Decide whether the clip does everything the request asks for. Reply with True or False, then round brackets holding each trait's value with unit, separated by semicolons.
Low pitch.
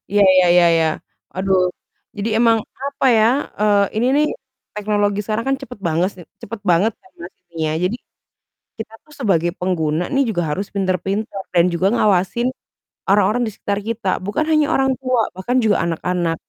False (205 Hz)